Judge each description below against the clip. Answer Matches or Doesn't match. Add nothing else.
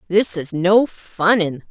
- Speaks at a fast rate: Doesn't match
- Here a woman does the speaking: Matches